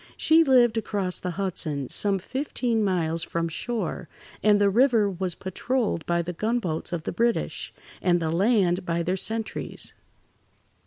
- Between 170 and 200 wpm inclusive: No, average, 150 wpm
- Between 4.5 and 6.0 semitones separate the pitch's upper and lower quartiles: Yes, average, 4.8 semitones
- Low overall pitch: No, high, 190 Hz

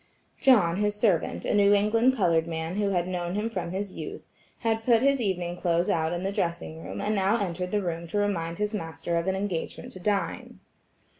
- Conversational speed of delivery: No, fast, 210 wpm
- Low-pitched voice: No, high, 190 Hz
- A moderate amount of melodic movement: Yes, average, 3.5 semitones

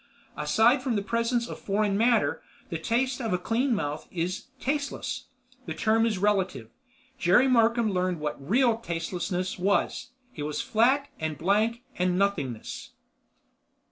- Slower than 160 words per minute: Yes, slow, 135 wpm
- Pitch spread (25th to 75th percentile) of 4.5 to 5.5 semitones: Yes, average, 4.8 semitones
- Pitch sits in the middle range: No, high, 210 Hz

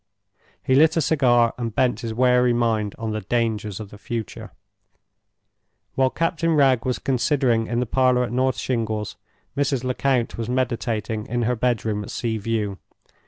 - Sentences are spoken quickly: No, average, 165 wpm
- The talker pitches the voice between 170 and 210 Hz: No, low, 120 Hz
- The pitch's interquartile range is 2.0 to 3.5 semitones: Yes, narrow, 2.6 semitones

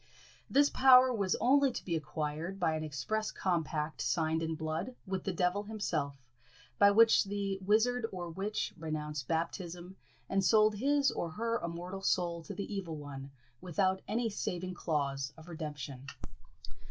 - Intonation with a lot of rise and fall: No, average, 4.8 semitones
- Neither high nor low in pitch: Yes, medium, 180 Hz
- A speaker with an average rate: Yes, average, 155 wpm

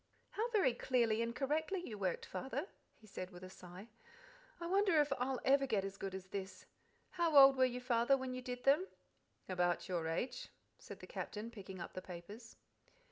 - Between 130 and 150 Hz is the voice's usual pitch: No, high, 235 Hz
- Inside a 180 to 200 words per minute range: Yes, average, 190 wpm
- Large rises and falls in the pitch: Yes, wide, 6.1 semitones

